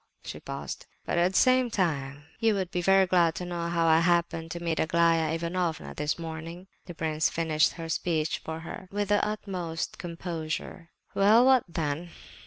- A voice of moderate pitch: Yes, medium, 170 Hz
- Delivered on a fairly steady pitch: Yes, narrow, 2.3 semitones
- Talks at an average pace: Yes, average, 180 wpm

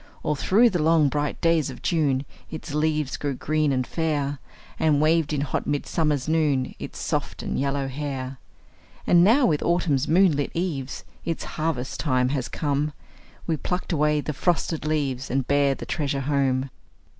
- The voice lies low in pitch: No, medium, 150 Hz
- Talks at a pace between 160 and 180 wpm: Yes, average, 170 wpm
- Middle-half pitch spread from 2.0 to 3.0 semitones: Yes, average, 2.7 semitones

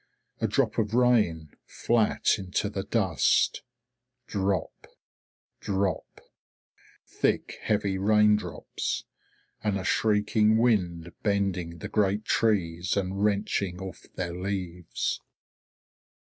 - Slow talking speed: Yes, slow, 95 wpm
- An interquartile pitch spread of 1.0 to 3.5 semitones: Yes, average, 2.7 semitones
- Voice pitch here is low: Yes, low, 100 Hz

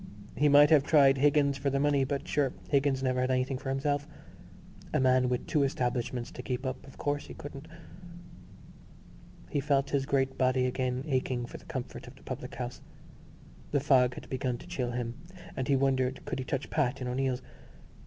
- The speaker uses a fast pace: No, average, 195 wpm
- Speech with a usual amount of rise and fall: No, narrow, 1.8 semitones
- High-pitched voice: No, low, 135 Hz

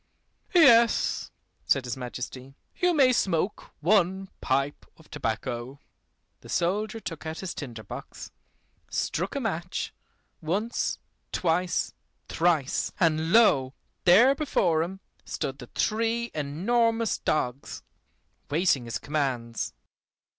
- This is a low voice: No, medium, 165 Hz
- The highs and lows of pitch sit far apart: Yes, wide, 7.8 semitones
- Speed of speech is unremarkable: No, slow, 110 wpm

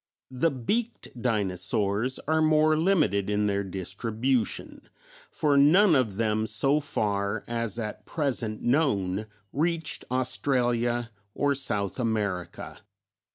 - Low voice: Yes, low, 120 Hz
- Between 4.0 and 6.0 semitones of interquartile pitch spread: Yes, wide, 5.6 semitones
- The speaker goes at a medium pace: No, slow, 110 wpm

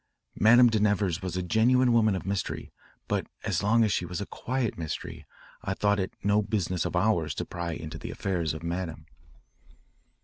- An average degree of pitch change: Yes, average, 3.9 semitones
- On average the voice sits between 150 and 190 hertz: No, low, 100 Hz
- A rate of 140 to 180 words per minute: No, average, 190 wpm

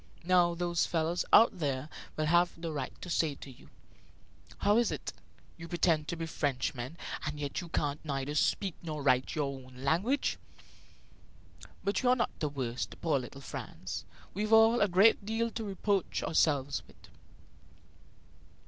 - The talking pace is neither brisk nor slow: Yes, average, 160 wpm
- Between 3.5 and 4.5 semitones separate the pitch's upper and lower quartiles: No, average, 5.3 semitones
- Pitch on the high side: No, medium, 165 Hz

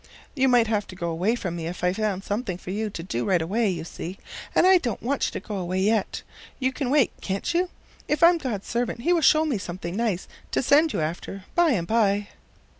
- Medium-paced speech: No, fast, 240 wpm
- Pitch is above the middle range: Yes, high, 210 Hz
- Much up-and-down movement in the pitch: Yes, wide, 6.0 semitones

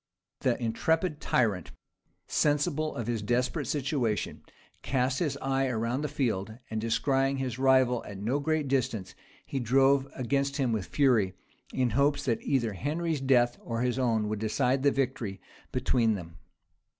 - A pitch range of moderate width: Yes, average, 3.4 semitones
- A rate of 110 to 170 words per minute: Yes, average, 150 wpm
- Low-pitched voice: Yes, low, 125 Hz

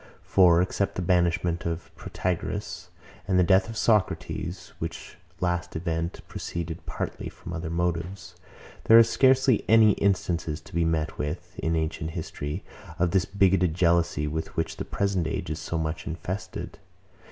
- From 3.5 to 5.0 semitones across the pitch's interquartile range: No, narrow, 2.5 semitones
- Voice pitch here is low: Yes, very low, 85 Hz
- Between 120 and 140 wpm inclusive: No, average, 150 wpm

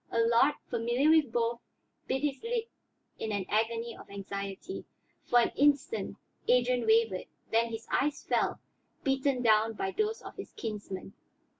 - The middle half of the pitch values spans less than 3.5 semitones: No, average, 4.1 semitones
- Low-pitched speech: No, high, 235 Hz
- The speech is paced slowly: No, average, 145 wpm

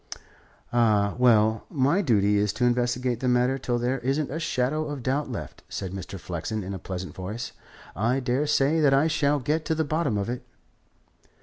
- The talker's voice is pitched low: Yes, low, 125 Hz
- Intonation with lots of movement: No, average, 4.9 semitones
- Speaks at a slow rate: No, average, 185 wpm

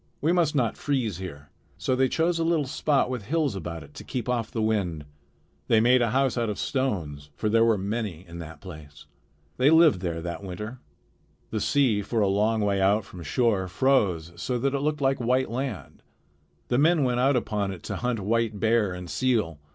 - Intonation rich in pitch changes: Yes, wide, 5.7 semitones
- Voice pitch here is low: Yes, low, 115 Hz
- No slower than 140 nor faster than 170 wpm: No, fast, 205 wpm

